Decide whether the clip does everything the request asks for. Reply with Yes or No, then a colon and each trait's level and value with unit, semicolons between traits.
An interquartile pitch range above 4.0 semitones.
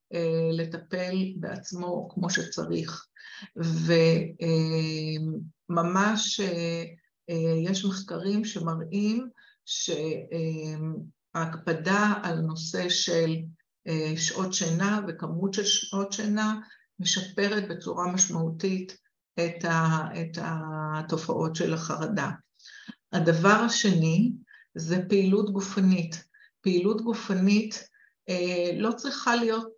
No: average, 3.6 semitones